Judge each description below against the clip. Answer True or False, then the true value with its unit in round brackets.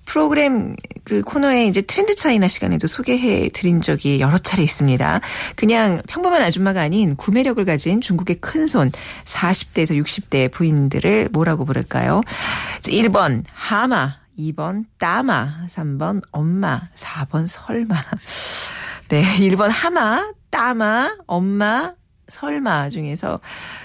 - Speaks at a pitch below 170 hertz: False (190 Hz)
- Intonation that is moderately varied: False (6.7 semitones)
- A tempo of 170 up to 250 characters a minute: True (245 characters per minute)